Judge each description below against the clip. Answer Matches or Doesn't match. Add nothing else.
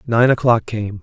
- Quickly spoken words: Doesn't match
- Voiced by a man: Matches